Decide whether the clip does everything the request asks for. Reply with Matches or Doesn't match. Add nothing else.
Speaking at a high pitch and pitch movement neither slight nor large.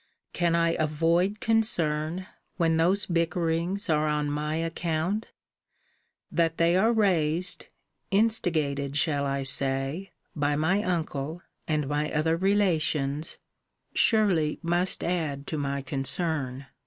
Doesn't match